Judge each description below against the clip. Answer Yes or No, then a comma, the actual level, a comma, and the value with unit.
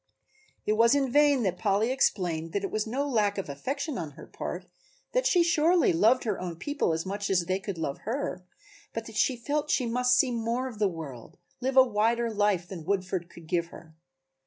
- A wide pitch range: Yes, wide, 6.0 semitones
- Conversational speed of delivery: No, fast, 210 wpm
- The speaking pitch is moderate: No, high, 215 Hz